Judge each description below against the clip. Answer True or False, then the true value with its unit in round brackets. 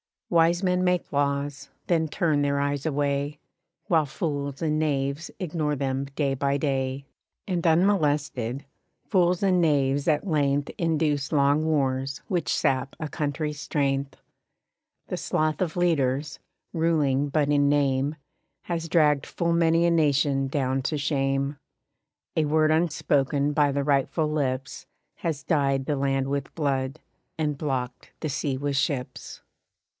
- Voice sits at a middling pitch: True (145 Hz)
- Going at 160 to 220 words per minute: False (140 wpm)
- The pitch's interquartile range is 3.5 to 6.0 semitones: False (2.5 semitones)